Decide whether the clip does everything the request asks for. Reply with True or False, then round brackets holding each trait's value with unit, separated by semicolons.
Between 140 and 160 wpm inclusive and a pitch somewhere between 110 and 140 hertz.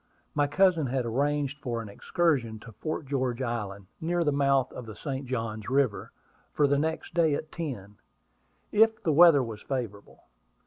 False (170 wpm; 135 Hz)